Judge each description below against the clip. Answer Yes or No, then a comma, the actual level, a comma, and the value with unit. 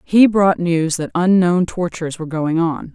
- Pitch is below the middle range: No, medium, 175 Hz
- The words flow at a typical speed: Yes, average, 185 wpm